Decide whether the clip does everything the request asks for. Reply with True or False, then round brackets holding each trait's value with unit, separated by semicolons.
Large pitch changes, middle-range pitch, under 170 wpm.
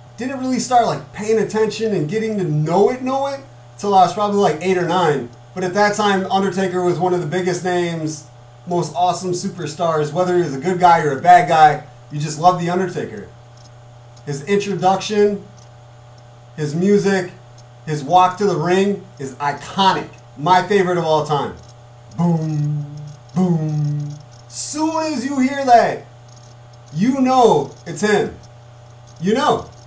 True (6.5 semitones; 175 Hz; 160 wpm)